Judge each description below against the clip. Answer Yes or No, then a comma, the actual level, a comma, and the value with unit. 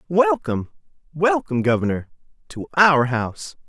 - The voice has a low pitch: Yes, low, 130 Hz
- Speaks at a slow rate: Yes, slow, 100 wpm